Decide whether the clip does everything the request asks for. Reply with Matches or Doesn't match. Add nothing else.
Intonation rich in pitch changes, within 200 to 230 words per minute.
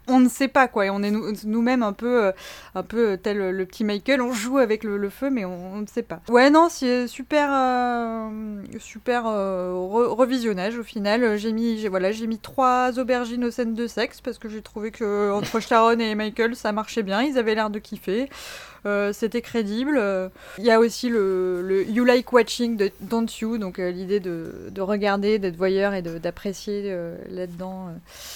Doesn't match